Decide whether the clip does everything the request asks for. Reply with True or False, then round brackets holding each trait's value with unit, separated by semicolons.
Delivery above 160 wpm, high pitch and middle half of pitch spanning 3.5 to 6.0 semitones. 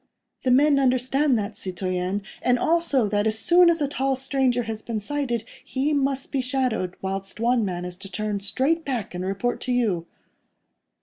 True (180 wpm; 245 Hz; 5.2 semitones)